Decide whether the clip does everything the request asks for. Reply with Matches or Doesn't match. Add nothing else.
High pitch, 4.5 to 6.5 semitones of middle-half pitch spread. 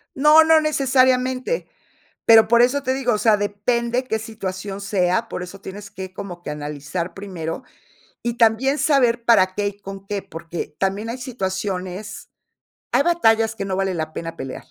Matches